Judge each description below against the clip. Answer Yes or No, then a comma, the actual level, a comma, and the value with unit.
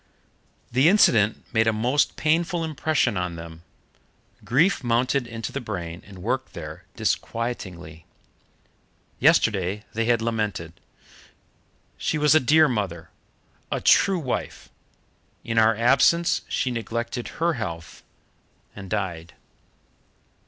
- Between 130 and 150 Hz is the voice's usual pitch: No, low, 115 Hz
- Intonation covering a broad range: Yes, wide, 6.2 semitones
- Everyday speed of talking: No, slow, 115 wpm